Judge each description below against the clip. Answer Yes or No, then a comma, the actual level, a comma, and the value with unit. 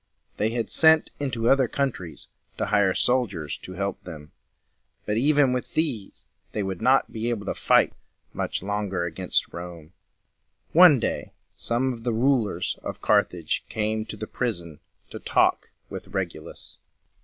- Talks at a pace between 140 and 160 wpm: Yes, average, 150 wpm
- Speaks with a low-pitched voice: Yes, low, 110 Hz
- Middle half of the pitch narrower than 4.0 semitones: No, average, 5.3 semitones